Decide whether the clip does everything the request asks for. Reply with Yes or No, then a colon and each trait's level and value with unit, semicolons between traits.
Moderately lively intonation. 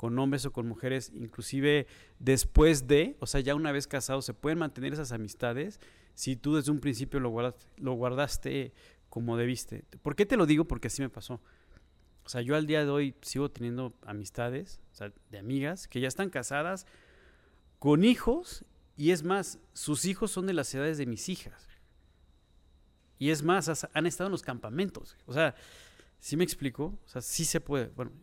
Yes: average, 4.4 semitones